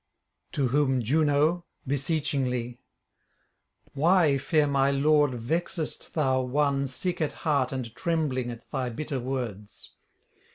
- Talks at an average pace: No, slow, 115 wpm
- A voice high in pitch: No, medium, 140 Hz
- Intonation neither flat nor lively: Yes, average, 3.2 semitones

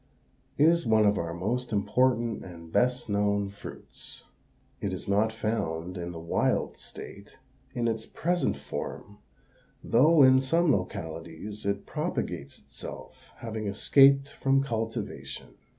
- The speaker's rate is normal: No, slow, 130 wpm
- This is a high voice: No, low, 110 Hz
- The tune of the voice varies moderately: Yes, average, 4.7 semitones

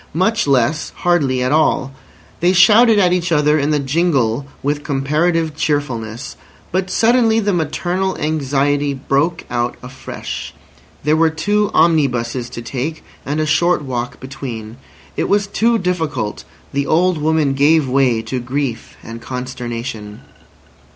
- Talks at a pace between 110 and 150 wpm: Yes, slow, 135 wpm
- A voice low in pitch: No, medium, 145 Hz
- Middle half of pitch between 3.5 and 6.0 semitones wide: Yes, average, 4.9 semitones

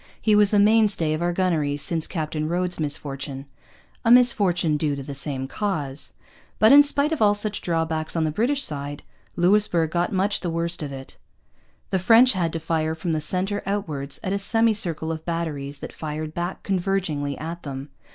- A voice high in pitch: No, medium, 170 Hz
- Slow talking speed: No, average, 185 wpm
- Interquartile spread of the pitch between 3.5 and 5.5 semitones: Yes, average, 4.8 semitones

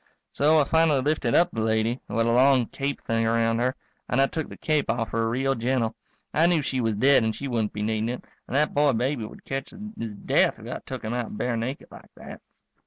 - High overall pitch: No, low, 125 Hz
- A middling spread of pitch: Yes, average, 3.7 semitones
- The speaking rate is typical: No, fast, 245 wpm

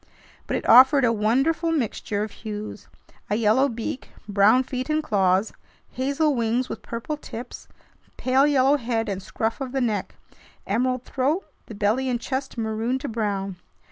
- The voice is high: Yes, high, 240 Hz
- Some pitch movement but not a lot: Yes, average, 3.7 semitones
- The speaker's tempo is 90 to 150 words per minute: No, average, 160 wpm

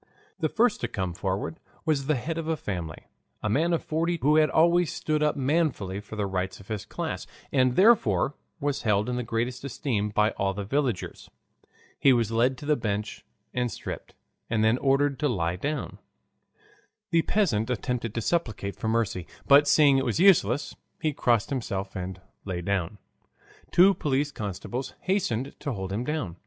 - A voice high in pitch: No, low, 125 Hz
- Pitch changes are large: Yes, wide, 6.4 semitones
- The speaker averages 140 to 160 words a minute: No, average, 180 wpm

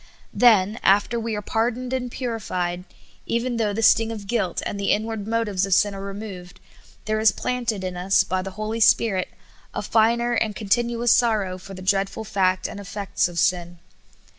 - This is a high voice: Yes, high, 210 Hz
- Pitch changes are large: No, average, 3.3 semitones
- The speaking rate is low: No, average, 180 wpm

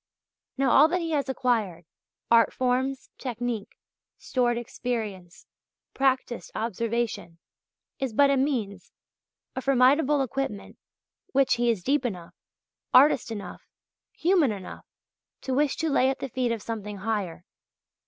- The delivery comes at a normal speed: No, slow, 130 wpm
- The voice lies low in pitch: No, high, 245 Hz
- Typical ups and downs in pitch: Yes, average, 3.8 semitones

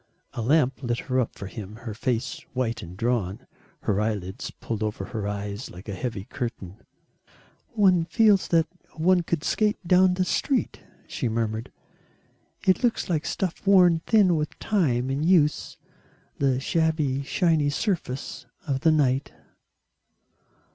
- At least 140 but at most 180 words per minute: Yes, average, 145 wpm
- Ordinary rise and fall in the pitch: No, wide, 7.4 semitones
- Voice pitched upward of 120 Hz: Yes, low, 135 Hz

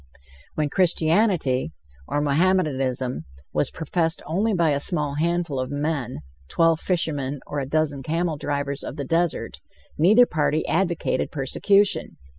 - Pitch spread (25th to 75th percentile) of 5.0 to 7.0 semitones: No, average, 3.4 semitones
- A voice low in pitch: No, medium, 155 Hz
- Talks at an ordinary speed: No, slow, 130 wpm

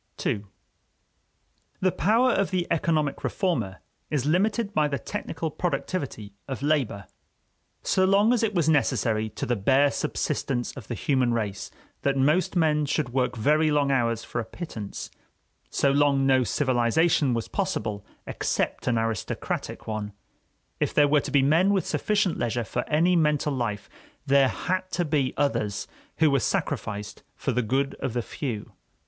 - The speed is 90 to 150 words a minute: No, average, 160 wpm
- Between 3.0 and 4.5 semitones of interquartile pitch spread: No, wide, 5.5 semitones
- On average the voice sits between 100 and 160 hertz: Yes, medium, 140 Hz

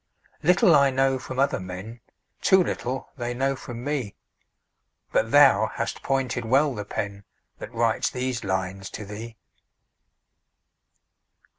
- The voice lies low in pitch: Yes, low, 120 Hz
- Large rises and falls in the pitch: No, average, 4.3 semitones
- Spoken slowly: Yes, slow, 130 wpm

